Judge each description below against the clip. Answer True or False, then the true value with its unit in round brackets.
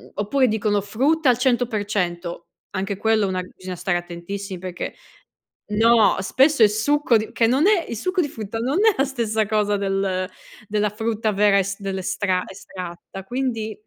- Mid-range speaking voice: False (210 Hz)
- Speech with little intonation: False (3.5 semitones)